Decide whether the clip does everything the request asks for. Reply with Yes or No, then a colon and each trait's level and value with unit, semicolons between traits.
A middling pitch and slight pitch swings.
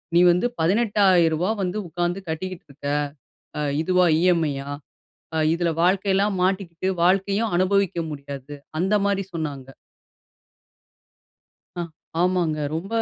No: medium, 180 Hz; average, 3.2 semitones